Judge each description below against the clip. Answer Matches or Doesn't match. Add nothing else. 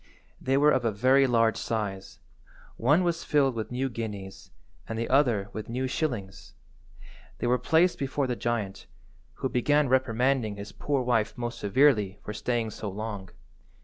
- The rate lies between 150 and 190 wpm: Matches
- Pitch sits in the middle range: Doesn't match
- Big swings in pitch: Doesn't match